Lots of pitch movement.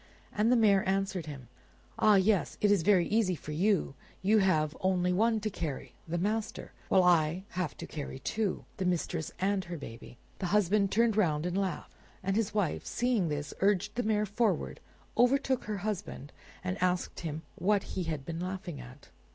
No: average, 3.9 semitones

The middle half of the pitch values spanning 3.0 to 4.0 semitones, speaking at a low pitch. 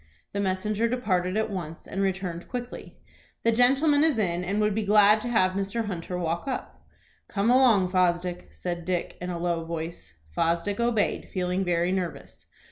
No: average, 3.7 semitones; high, 190 Hz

